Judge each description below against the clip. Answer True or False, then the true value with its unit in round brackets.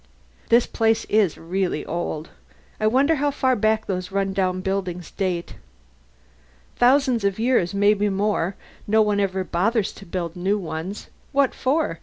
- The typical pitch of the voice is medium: False (200 Hz)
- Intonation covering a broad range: False (3.5 semitones)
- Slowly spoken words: False (145 wpm)